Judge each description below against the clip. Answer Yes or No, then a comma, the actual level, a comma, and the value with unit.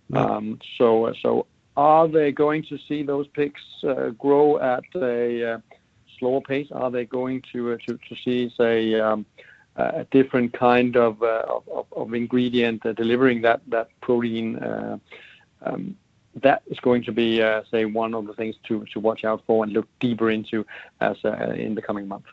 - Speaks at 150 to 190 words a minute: Yes, average, 185 wpm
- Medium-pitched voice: No, low, 120 Hz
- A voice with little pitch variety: Yes, narrow, 2.2 semitones